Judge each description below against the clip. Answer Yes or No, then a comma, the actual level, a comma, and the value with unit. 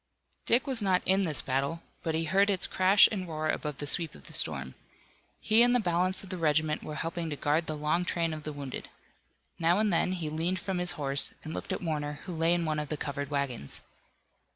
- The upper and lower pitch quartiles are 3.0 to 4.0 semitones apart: Yes, average, 3.5 semitones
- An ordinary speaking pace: No, fast, 230 wpm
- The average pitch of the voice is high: No, medium, 165 Hz